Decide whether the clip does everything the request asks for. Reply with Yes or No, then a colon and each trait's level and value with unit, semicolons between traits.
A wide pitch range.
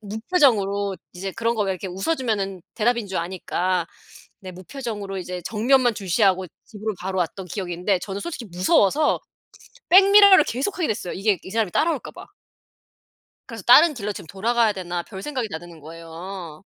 No: average, 4.3 semitones